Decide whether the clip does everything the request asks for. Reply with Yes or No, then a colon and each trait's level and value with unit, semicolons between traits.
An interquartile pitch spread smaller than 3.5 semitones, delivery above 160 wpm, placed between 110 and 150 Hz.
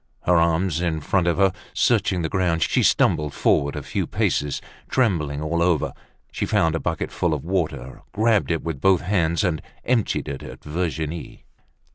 No: average, 2.9 semitones; average, 175 wpm; very low, 85 Hz